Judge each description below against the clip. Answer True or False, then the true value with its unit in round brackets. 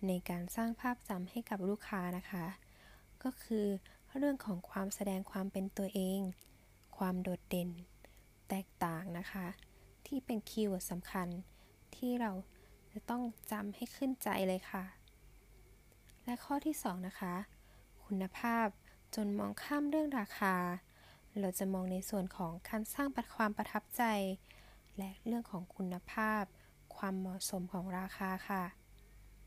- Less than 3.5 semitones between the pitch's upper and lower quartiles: True (3.1 semitones)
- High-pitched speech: True (195 Hz)